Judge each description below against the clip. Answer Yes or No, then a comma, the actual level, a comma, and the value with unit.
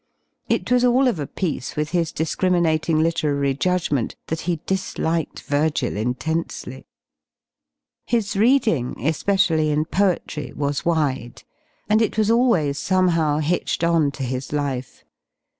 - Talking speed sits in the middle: No, slow, 125 wpm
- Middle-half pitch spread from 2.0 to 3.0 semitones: No, average, 4.3 semitones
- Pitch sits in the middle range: Yes, medium, 160 Hz